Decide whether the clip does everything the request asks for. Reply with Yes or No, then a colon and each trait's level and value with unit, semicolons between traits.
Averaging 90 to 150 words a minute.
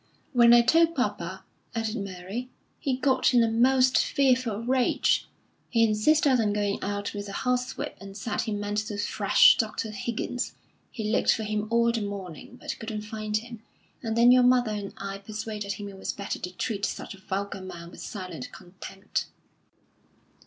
No: average, 175 wpm